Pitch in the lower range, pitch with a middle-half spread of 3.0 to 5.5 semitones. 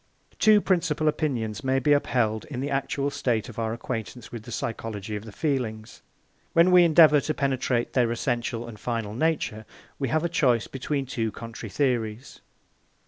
Yes: low, 125 Hz; average, 4.3 semitones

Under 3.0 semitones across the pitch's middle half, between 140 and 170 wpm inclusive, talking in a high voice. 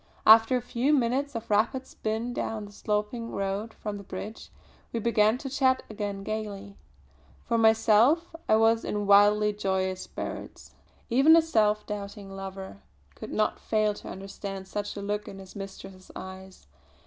Yes: narrow, 2.5 semitones; average, 160 wpm; high, 210 Hz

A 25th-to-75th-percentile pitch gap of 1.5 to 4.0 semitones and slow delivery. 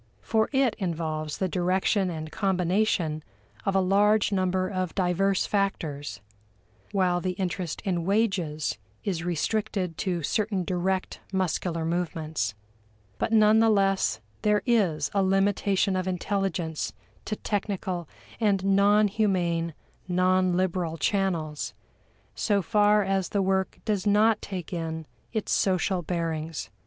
Yes: average, 2.9 semitones; slow, 125 wpm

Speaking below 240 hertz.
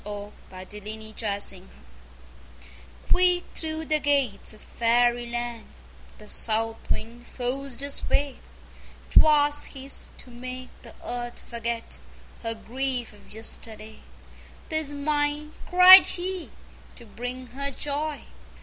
No: high, 245 Hz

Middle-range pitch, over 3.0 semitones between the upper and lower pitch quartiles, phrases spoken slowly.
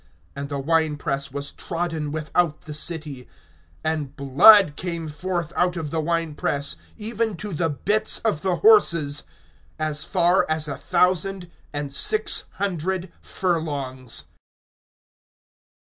Yes: medium, 160 Hz; average, 3.6 semitones; slow, 130 wpm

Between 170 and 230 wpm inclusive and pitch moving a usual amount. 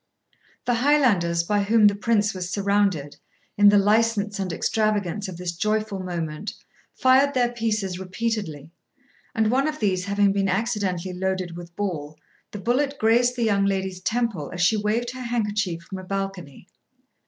No: average, 160 wpm; average, 3.6 semitones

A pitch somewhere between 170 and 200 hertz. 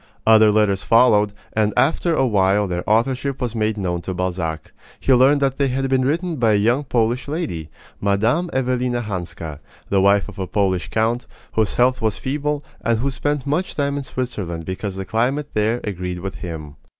No: low, 110 Hz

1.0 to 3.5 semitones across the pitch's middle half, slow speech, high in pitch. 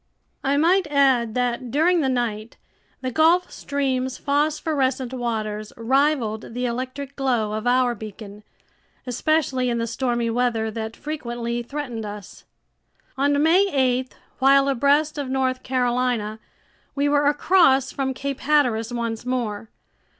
Yes: average, 3.2 semitones; slow, 130 wpm; very high, 255 Hz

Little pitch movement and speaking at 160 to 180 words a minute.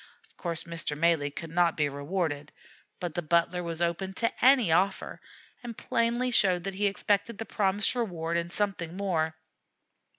No: average, 3.4 semitones; average, 165 wpm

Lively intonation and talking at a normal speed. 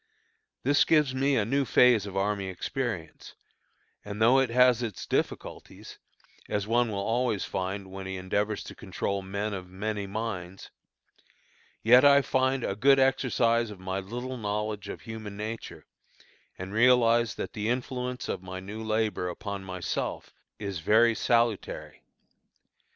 No: average, 3.8 semitones; average, 145 wpm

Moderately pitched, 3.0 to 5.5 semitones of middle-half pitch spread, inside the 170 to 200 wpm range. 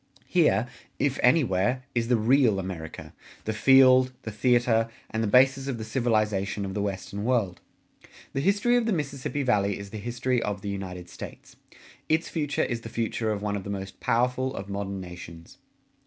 No: low, 115 Hz; average, 4.4 semitones; average, 180 wpm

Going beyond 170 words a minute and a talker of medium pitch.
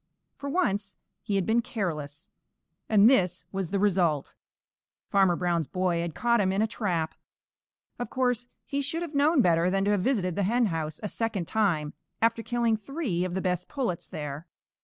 No: average, 180 wpm; high, 195 Hz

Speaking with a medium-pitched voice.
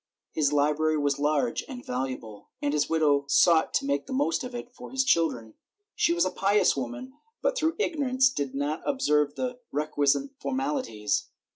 Yes: medium, 155 Hz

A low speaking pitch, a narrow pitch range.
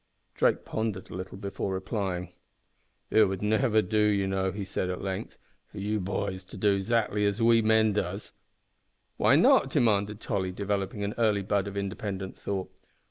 Yes: low, 100 Hz; narrow, 1.9 semitones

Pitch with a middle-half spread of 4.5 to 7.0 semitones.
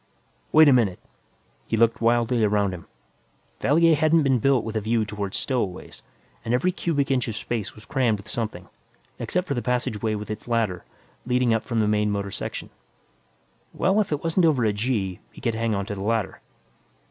No: average, 4.1 semitones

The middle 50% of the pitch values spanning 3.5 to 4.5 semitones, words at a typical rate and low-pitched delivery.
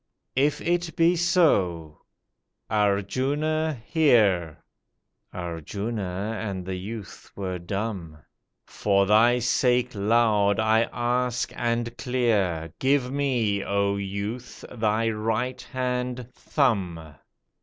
No: average, 4.2 semitones; slow, 95 wpm; low, 110 Hz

